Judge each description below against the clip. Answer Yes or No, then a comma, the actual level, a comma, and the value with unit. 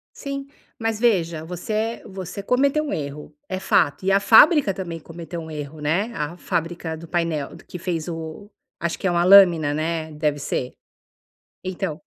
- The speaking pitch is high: No, medium, 170 Hz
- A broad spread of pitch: No, average, 3.9 semitones